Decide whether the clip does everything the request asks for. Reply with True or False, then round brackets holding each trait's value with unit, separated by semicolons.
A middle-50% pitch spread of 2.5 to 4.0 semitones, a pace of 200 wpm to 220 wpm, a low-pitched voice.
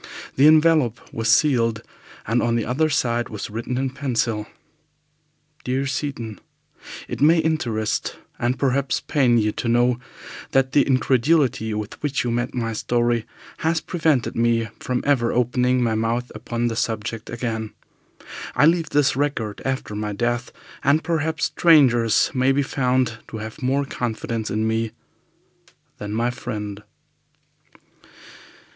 False (3.3 semitones; 140 wpm; 120 Hz)